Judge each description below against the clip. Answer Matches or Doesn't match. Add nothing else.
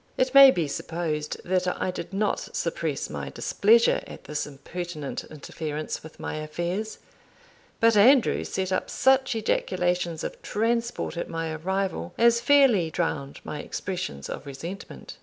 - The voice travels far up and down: Matches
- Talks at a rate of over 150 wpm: Doesn't match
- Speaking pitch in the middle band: Matches